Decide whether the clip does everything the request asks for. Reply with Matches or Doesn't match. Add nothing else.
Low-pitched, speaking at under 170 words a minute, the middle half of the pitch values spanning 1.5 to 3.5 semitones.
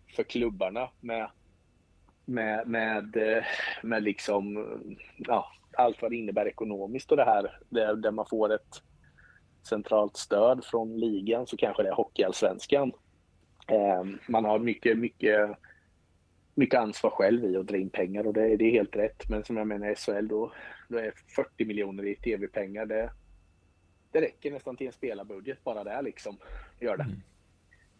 Matches